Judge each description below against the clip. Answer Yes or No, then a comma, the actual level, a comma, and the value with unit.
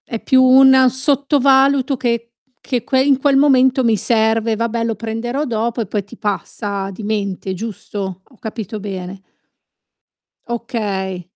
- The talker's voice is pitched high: Yes, high, 230 Hz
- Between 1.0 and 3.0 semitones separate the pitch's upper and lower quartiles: No, average, 4.1 semitones